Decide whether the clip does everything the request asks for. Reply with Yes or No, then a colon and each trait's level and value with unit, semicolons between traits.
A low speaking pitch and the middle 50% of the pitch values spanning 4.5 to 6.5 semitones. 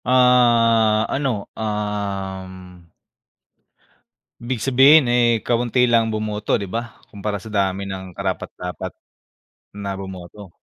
No: low, 105 Hz; average, 3.5 semitones